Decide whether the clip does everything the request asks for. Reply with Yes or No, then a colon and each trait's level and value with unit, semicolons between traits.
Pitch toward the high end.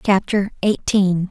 Yes: high, 195 Hz